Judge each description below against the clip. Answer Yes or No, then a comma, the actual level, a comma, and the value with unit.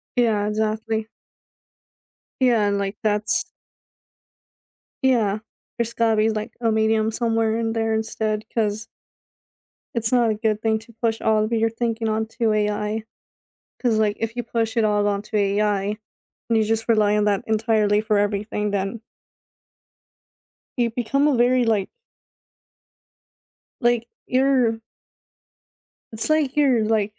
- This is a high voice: Yes, high, 220 Hz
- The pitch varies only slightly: Yes, narrow, 1.5 semitones